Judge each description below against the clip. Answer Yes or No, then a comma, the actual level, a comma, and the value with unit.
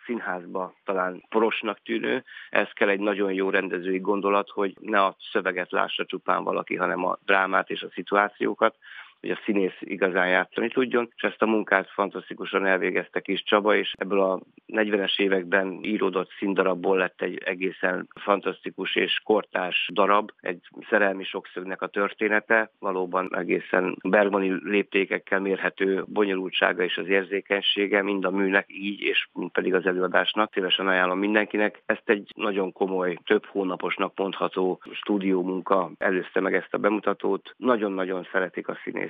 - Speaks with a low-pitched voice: Yes, very low, 95 Hz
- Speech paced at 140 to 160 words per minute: Yes, average, 145 wpm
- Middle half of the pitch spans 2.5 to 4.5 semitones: No, narrow, 1.5 semitones